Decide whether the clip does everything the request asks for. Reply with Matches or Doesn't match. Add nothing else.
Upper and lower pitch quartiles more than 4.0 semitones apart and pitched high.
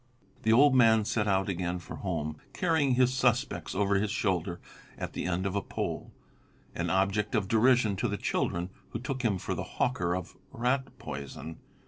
Doesn't match